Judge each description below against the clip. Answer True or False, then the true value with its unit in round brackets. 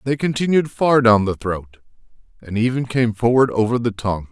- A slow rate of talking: False (180 wpm)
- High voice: False (120 Hz)